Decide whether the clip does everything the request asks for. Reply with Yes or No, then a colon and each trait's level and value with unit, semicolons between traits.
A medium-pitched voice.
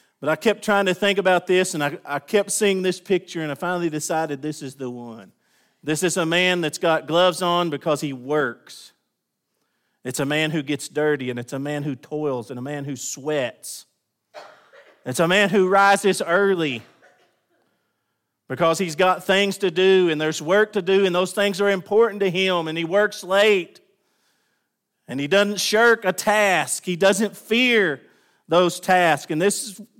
Yes: medium, 180 Hz